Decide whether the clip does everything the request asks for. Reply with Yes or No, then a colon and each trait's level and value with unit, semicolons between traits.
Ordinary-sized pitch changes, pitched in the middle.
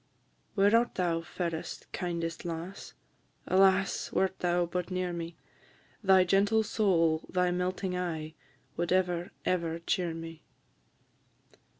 No: narrow, 2.1 semitones; medium, 180 Hz